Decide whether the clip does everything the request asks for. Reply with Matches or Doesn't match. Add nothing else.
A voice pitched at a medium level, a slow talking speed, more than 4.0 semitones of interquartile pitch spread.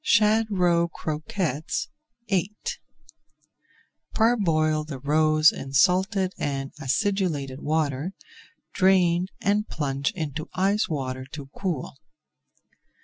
Matches